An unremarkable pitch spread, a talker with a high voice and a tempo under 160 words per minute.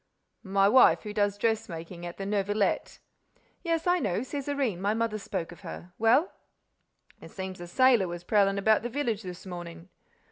Yes: average, 4.2 semitones; high, 205 Hz; average, 150 wpm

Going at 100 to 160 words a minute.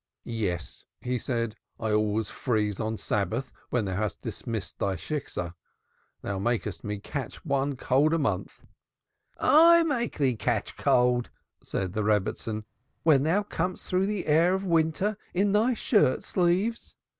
Yes: average, 150 wpm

